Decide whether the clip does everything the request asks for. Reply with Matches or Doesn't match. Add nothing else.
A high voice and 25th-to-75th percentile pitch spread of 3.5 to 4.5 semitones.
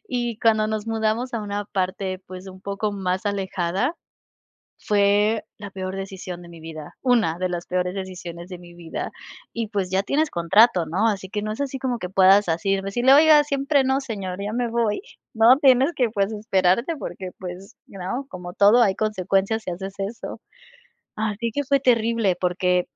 Matches